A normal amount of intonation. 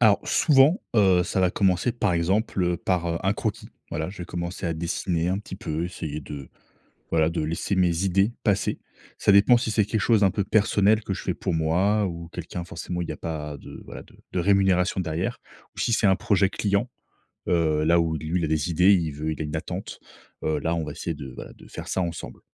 Yes: average, 3.4 semitones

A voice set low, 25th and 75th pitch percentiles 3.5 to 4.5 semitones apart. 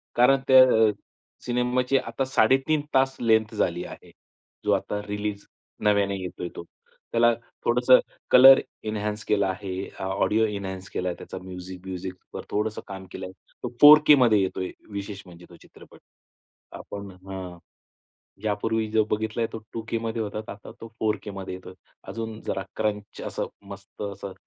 No: low, 105 Hz; average, 3.1 semitones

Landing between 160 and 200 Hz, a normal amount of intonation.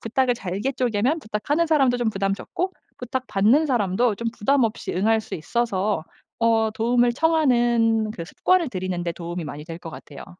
No: high, 225 Hz; average, 4.4 semitones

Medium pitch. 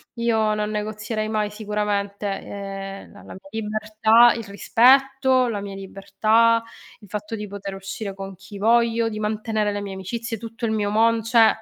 No: high, 215 Hz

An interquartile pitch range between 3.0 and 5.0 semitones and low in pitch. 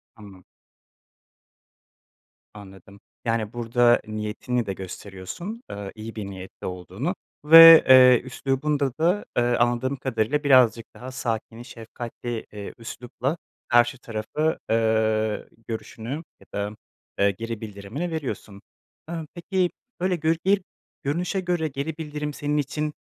No: wide, 5.6 semitones; low, 120 Hz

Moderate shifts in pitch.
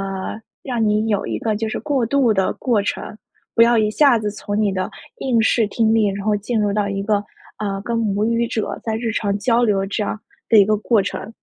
No: narrow, 2.2 semitones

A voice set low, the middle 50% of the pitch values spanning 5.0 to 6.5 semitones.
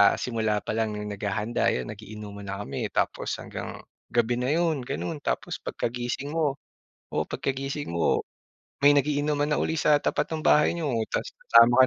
Yes: low, 125 Hz; wide, 5.5 semitones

